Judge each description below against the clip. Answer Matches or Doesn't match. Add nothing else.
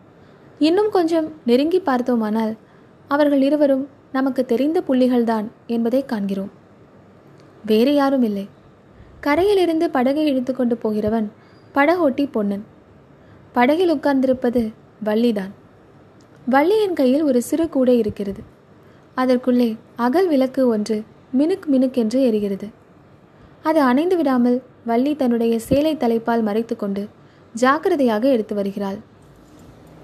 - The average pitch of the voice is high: Matches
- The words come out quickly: Doesn't match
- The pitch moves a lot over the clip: Doesn't match